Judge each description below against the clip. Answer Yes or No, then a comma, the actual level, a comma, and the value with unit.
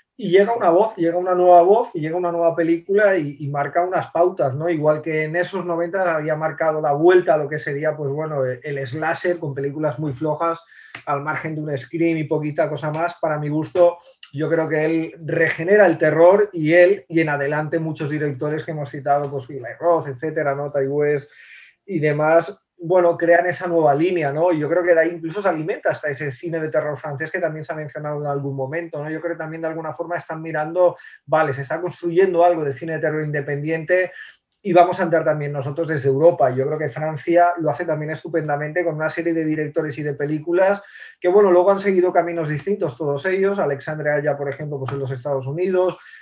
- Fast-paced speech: Yes, fast, 220 wpm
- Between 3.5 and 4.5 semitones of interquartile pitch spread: No, narrow, 2.6 semitones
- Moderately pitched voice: Yes, medium, 160 Hz